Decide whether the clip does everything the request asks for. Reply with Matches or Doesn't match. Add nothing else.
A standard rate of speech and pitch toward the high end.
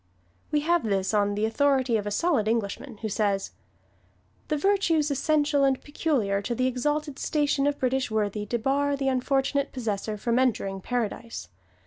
Matches